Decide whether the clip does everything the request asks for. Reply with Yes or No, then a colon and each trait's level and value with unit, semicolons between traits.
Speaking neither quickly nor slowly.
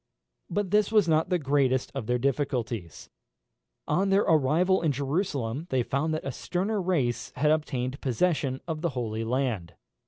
Yes: average, 160 wpm